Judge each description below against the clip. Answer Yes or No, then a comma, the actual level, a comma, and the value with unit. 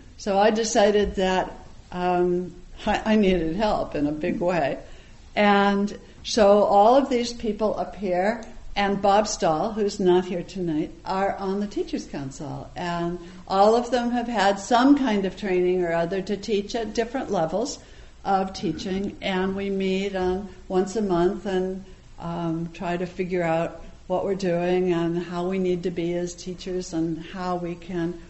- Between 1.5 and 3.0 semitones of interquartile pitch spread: Yes, narrow, 2.5 semitones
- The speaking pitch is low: No, high, 190 Hz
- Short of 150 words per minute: No, average, 170 wpm